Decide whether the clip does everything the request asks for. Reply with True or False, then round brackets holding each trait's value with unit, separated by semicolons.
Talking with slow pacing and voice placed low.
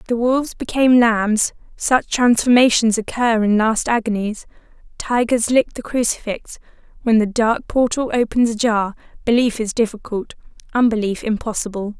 False (120 wpm; 230 Hz)